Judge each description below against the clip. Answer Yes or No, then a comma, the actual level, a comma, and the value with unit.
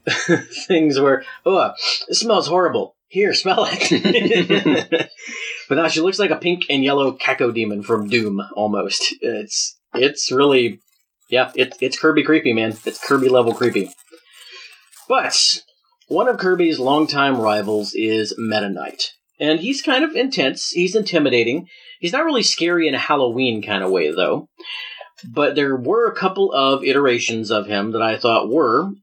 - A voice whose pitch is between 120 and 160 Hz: Yes, medium, 140 Hz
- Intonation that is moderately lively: No, wide, 8.2 semitones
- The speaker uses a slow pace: No, average, 155 wpm